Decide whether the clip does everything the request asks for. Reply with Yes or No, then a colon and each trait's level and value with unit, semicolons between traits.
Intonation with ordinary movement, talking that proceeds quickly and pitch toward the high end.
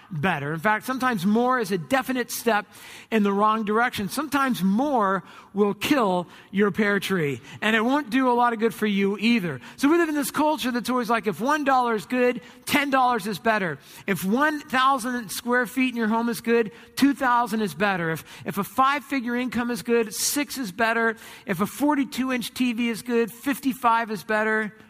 Yes: average, 3.6 semitones; fast, 210 wpm; high, 235 Hz